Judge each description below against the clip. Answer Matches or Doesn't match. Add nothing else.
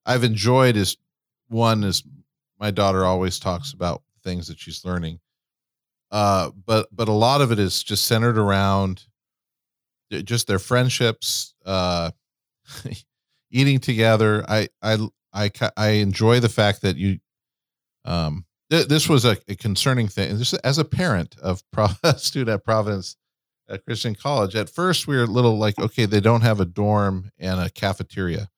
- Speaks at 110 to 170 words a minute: Matches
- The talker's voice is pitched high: Doesn't match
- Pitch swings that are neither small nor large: Matches